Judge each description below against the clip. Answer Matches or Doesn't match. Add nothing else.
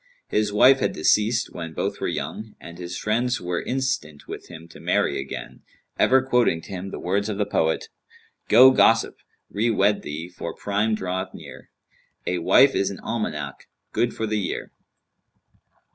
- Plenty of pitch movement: Doesn't match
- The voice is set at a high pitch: Doesn't match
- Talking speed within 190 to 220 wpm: Doesn't match